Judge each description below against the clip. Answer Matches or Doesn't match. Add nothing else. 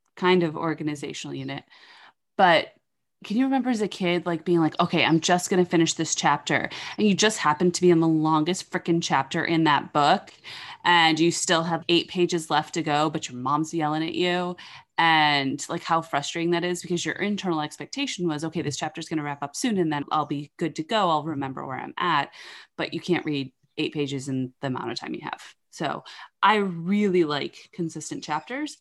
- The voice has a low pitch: Doesn't match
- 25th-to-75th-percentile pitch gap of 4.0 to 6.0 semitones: Doesn't match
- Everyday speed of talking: Doesn't match